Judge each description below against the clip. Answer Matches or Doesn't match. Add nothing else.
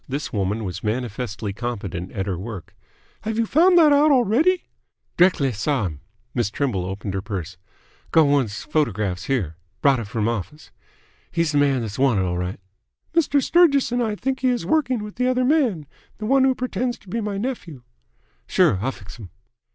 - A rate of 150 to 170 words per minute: Doesn't match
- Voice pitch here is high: Doesn't match